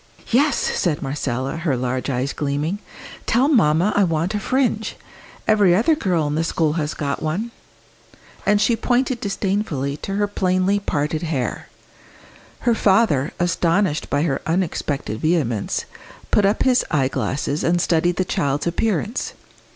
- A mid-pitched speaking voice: Yes, medium, 170 Hz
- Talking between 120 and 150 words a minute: Yes, average, 145 wpm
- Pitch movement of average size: No, wide, 5.9 semitones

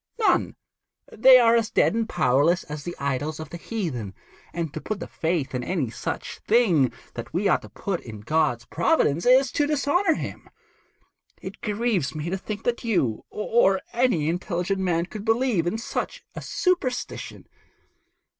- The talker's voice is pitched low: No, medium, 185 Hz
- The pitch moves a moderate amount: No, wide, 7.1 semitones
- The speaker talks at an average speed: Yes, average, 170 wpm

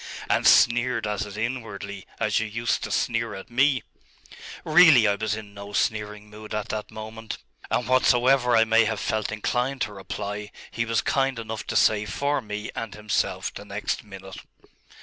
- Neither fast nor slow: Yes, average, 175 wpm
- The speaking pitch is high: No, low, 110 Hz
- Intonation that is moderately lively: No, narrow, 2.3 semitones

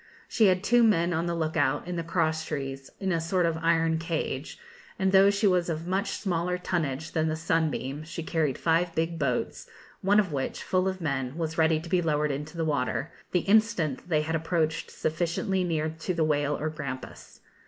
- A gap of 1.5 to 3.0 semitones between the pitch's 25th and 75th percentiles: Yes, average, 2.7 semitones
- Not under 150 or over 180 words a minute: No, fast, 205 wpm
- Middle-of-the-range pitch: Yes, medium, 165 Hz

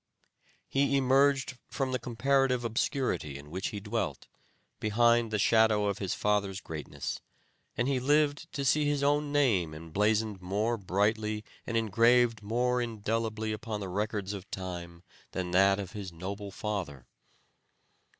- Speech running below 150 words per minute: Yes, average, 140 wpm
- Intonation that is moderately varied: Yes, average, 4.2 semitones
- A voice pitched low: Yes, low, 110 Hz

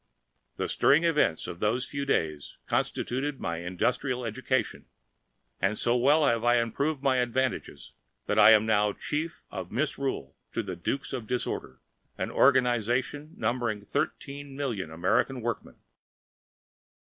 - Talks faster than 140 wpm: No, slow, 135 wpm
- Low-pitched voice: Yes, low, 120 Hz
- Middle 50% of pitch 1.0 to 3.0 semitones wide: No, average, 4.6 semitones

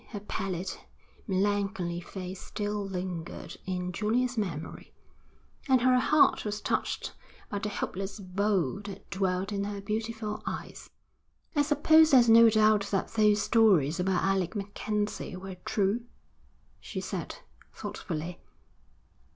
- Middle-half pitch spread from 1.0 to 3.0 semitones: Yes, narrow, 2.6 semitones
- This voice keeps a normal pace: No, slow, 125 wpm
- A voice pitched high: Yes, high, 200 Hz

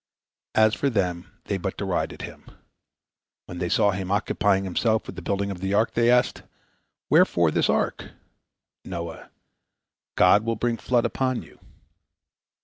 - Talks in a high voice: No, low, 100 Hz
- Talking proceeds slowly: No, average, 150 wpm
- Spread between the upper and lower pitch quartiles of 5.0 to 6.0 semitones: No, average, 3.7 semitones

